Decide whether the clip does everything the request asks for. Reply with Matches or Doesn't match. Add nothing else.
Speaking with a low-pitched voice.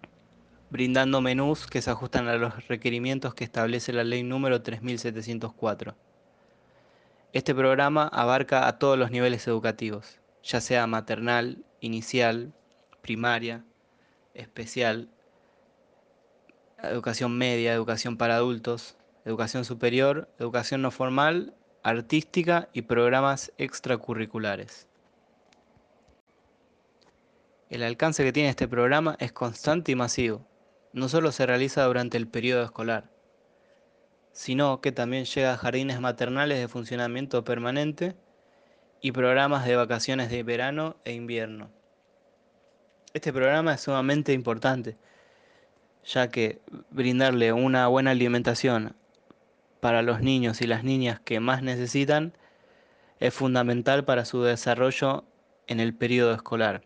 Matches